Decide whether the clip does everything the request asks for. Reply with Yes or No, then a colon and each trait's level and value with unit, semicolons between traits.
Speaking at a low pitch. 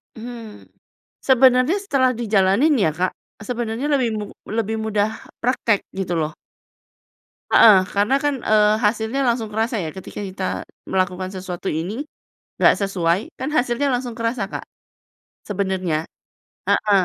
No: high, 220 Hz